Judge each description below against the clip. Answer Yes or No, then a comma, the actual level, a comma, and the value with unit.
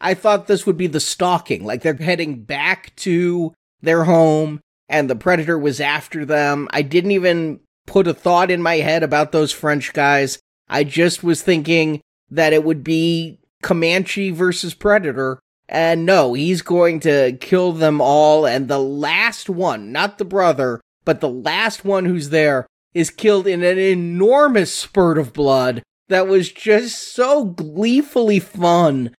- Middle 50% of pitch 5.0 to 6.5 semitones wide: No, average, 3.7 semitones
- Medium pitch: Yes, medium, 165 Hz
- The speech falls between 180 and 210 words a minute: No, average, 160 wpm